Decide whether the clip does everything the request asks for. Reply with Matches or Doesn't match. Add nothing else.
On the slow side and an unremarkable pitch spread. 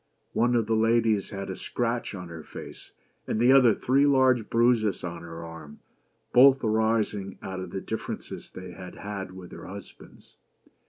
Doesn't match